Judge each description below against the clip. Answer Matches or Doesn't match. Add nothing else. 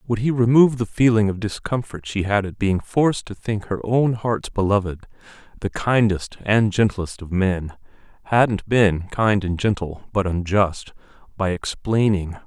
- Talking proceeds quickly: Doesn't match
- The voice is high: Doesn't match